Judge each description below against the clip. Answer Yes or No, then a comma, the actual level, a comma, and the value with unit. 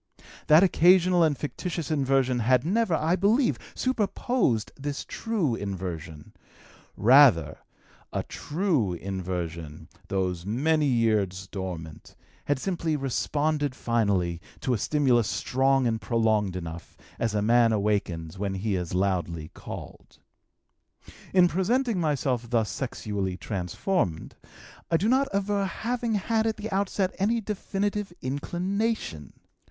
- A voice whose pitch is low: Yes, low, 130 Hz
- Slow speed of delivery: Yes, slow, 120 wpm